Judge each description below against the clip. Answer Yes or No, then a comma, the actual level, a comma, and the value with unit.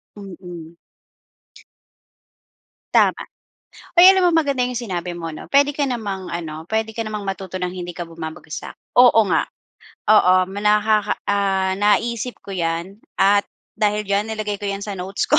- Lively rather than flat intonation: No, average, 3.5 semitones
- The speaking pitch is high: Yes, high, 200 Hz